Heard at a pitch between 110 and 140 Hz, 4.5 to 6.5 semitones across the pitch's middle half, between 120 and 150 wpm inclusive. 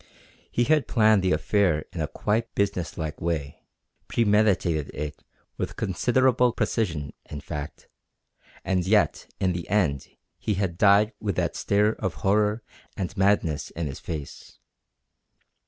No: very low, 95 Hz; average, 4.8 semitones; average, 140 wpm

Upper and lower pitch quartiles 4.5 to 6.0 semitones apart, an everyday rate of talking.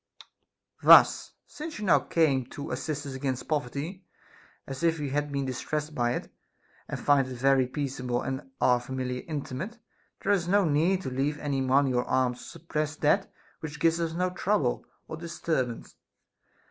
No: average, 4.0 semitones; average, 170 wpm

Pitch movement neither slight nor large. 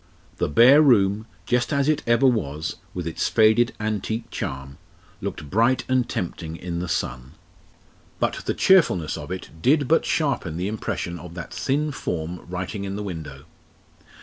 No: wide, 6.6 semitones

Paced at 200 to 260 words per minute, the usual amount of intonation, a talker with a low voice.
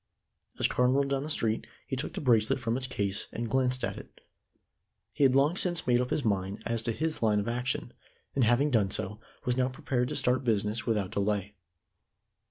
Yes: fast, 205 wpm; average, 3.6 semitones; low, 120 Hz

